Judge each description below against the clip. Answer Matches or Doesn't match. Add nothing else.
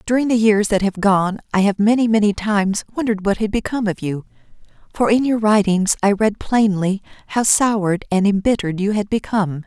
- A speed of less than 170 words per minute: Doesn't match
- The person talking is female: Matches